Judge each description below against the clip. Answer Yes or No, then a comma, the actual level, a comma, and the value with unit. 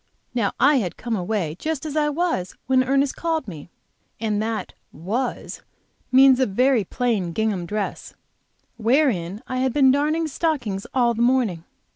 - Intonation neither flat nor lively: Yes, average, 5.0 semitones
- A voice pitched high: Yes, high, 245 Hz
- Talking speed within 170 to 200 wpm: No, average, 155 wpm